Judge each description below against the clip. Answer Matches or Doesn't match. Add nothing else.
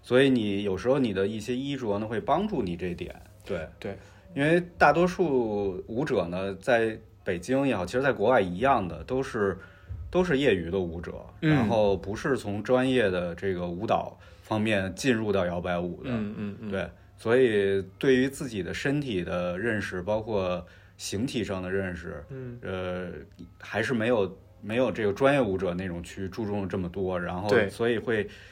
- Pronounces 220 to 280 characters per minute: Matches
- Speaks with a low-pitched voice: Matches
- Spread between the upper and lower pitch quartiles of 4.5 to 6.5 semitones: Matches